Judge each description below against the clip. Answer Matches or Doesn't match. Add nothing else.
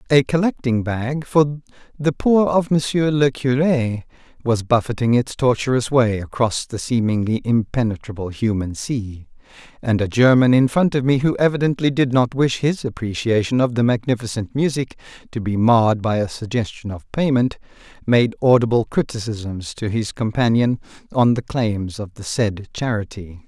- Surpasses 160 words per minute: Doesn't match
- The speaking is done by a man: Matches